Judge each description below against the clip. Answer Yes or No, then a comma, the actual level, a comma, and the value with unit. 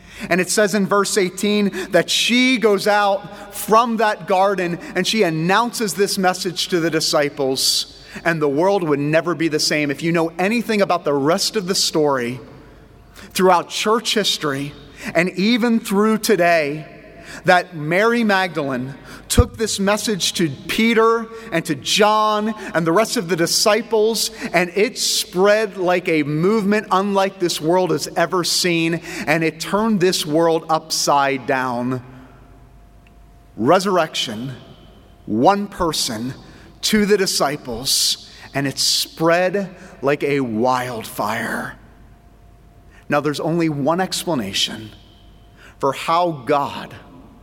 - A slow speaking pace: Yes, slow, 130 wpm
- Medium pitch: Yes, medium, 175 Hz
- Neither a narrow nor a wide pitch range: No, wide, 5.7 semitones